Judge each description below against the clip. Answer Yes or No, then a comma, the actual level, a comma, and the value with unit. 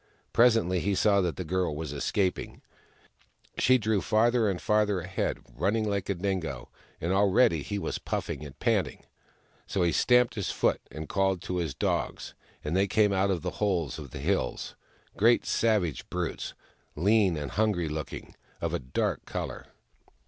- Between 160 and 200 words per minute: Yes, average, 170 wpm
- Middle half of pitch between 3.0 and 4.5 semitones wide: Yes, average, 4.0 semitones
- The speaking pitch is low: Yes, very low, 95 Hz